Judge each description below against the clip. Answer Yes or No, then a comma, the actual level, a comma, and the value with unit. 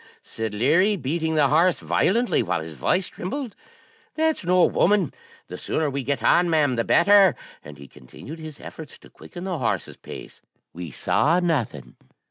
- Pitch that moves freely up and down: Yes, wide, 6.2 semitones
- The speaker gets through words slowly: No, average, 165 wpm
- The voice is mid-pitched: Yes, medium, 160 Hz